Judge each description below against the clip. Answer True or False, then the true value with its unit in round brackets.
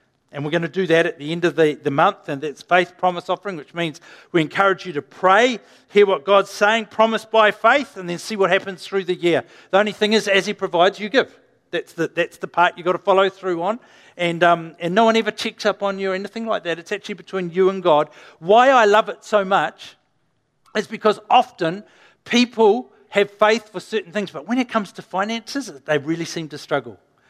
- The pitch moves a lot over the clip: False (3.7 semitones)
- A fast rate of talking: True (235 wpm)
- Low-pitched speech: False (190 Hz)